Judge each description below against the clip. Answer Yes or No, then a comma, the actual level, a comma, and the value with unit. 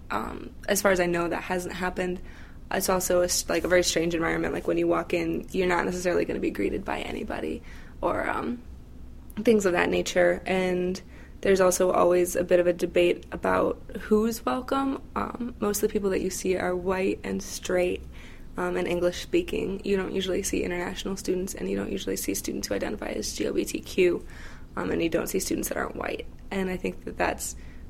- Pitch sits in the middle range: Yes, medium, 180 Hz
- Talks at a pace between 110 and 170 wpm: No, average, 200 wpm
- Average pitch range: No, narrow, 2.2 semitones